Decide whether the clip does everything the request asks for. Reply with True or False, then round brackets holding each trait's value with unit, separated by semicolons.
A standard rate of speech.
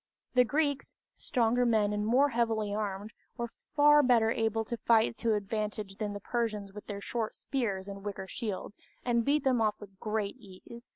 True (180 wpm)